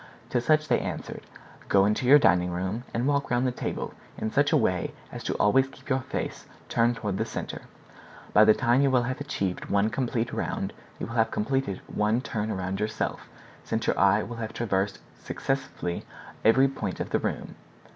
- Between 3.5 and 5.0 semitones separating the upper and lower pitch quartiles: Yes, average, 4.4 semitones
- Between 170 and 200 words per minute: Yes, average, 195 wpm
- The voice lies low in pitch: Yes, low, 115 Hz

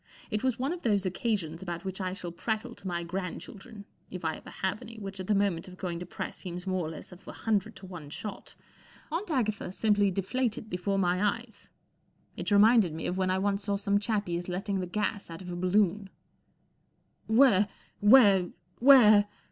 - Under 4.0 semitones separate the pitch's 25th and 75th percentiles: Yes, average, 2.9 semitones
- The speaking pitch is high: Yes, high, 195 Hz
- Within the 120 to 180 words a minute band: No, average, 195 wpm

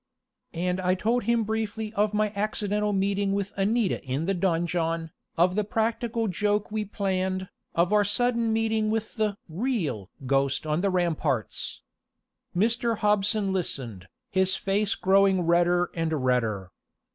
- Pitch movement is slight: No, average, 3.8 semitones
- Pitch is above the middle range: Yes, high, 195 Hz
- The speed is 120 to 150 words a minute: Yes, average, 140 wpm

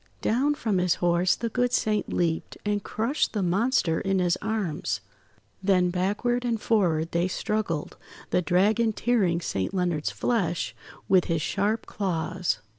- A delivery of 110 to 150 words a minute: Yes, average, 145 wpm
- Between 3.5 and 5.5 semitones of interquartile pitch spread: Yes, average, 4.0 semitones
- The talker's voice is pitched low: No, high, 190 Hz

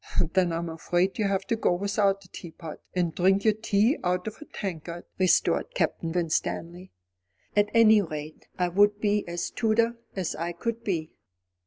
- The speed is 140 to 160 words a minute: No, average, 170 wpm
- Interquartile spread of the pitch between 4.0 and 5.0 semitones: No, average, 3.4 semitones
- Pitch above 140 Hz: Yes, high, 190 Hz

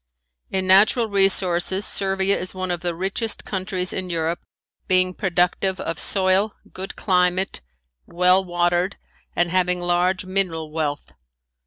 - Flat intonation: Yes, narrow, 1.5 semitones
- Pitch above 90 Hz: Yes, medium, 185 Hz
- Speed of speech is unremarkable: No, slow, 130 wpm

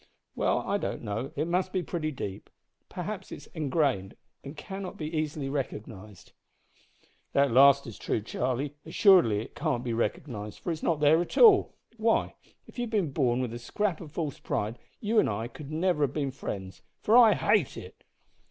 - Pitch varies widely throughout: Yes, wide, 6.2 semitones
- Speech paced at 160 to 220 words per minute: Yes, average, 190 wpm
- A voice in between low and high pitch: Yes, medium, 145 Hz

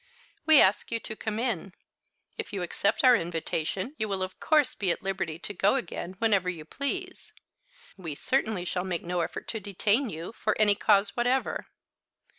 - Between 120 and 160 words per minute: No, average, 180 wpm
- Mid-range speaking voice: No, high, 200 Hz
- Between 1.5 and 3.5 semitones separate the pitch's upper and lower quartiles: No, average, 4.5 semitones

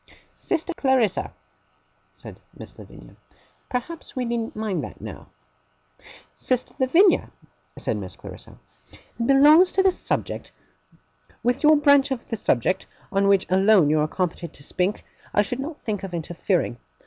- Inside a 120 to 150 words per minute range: Yes, average, 145 wpm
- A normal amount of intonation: No, wide, 6.9 semitones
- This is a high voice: Yes, high, 230 Hz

